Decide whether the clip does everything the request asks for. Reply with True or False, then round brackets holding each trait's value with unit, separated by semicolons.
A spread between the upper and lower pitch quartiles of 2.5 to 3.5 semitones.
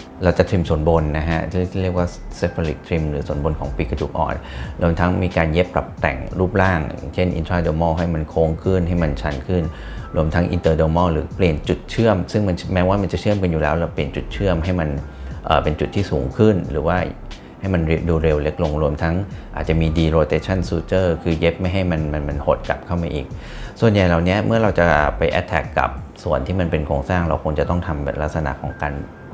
True (3.0 semitones)